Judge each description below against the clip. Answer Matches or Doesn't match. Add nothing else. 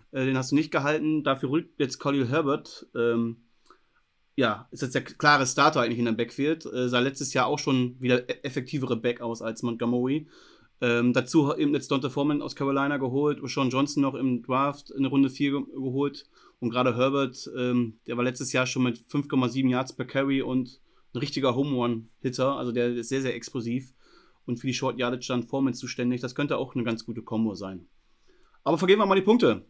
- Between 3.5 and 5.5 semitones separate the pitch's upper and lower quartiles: Doesn't match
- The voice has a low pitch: Matches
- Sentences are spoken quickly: Matches